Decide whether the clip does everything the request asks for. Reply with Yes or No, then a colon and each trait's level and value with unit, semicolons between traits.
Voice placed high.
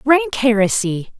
Yes: very high, 250 Hz